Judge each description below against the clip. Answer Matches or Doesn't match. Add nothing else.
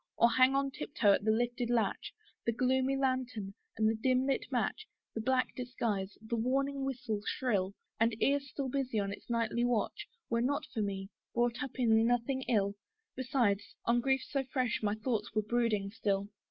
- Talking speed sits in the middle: Matches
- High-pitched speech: Matches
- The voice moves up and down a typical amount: Matches